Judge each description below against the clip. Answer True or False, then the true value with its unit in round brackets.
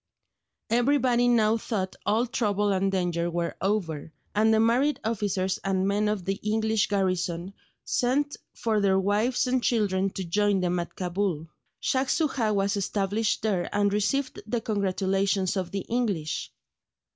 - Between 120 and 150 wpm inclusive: True (145 wpm)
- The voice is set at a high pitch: True (205 Hz)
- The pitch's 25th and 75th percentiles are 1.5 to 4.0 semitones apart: True (3.1 semitones)